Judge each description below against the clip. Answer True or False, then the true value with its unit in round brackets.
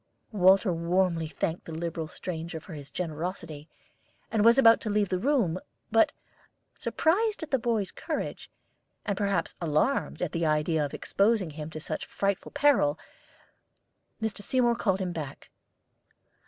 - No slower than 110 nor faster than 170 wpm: True (145 wpm)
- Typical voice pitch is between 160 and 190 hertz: True (185 Hz)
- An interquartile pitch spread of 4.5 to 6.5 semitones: True (5.5 semitones)